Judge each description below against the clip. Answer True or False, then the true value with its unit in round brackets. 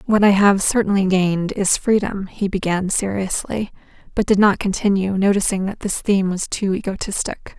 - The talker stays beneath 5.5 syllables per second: True (5.1 syllables/s)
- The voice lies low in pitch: False (195 Hz)